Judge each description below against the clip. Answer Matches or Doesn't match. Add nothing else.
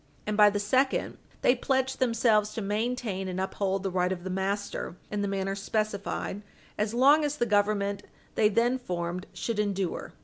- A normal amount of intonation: Matches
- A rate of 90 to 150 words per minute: Doesn't match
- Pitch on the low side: Doesn't match